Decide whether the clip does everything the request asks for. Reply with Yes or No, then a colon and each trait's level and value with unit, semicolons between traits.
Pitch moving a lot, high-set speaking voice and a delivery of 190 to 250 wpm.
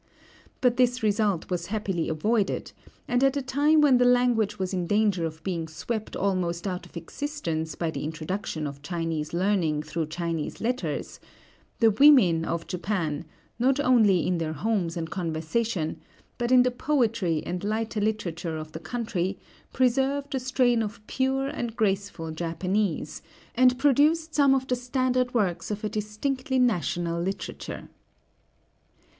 No: wide, 6.7 semitones; high, 205 Hz; average, 150 wpm